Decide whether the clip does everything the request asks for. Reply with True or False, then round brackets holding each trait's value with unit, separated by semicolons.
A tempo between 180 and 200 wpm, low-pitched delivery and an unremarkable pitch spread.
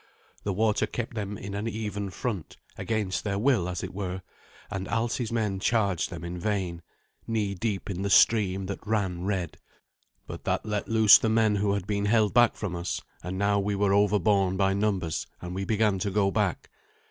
False (195 wpm; 100 Hz; 2.1 semitones)